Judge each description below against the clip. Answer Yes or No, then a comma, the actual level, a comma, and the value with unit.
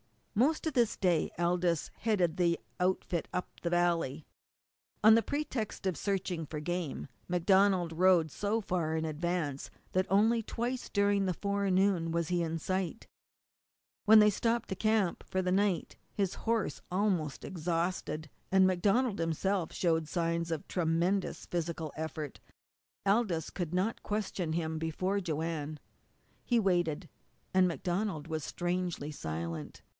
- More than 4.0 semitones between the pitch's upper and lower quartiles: No, average, 3.5 semitones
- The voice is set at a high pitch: No, medium, 180 Hz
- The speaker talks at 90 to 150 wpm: Yes, average, 140 wpm